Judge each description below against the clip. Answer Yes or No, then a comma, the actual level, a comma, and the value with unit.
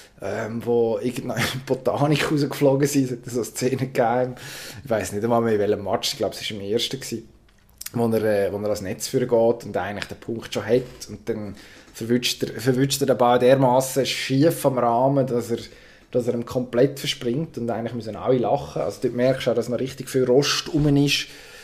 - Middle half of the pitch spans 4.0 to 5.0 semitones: No, narrow, 2.4 semitones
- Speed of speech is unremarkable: No, fast, 210 wpm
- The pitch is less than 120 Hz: No, low, 125 Hz